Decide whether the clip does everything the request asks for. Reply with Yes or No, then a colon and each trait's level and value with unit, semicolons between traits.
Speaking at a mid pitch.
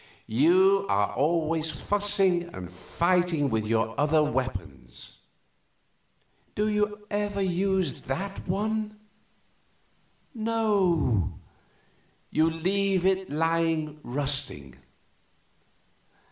Yes: medium, 175 Hz